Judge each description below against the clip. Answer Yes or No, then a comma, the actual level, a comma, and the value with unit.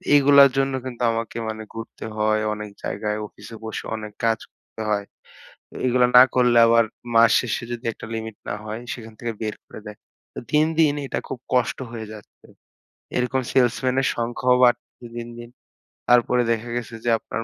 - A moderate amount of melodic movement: No, narrow, 2.1 semitones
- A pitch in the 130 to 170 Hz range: No, low, 120 Hz